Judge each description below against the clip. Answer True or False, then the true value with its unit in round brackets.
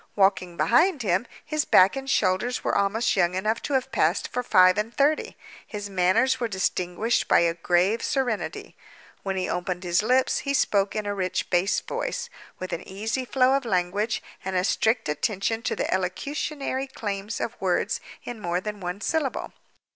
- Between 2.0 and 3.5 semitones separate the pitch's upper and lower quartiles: False (5.1 semitones)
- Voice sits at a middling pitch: False (205 Hz)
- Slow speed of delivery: False (175 wpm)